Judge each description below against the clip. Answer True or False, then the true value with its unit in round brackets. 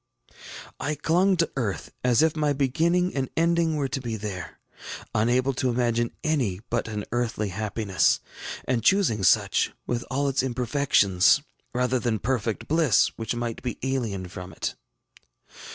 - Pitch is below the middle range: True (125 Hz)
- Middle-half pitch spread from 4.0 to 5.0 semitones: True (4.5 semitones)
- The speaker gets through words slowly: False (150 wpm)